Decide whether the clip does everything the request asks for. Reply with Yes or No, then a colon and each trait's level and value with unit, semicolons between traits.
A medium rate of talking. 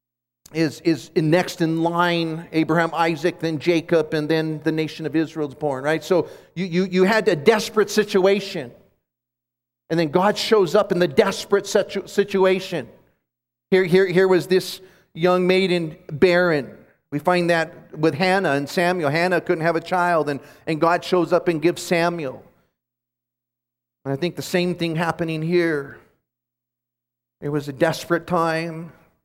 Yes: average, 160 wpm